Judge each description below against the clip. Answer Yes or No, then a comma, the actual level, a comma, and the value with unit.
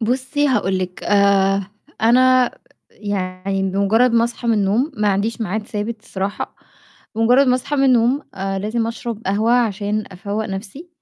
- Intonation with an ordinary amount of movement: Yes, average, 3.4 semitones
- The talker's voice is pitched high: Yes, high, 215 Hz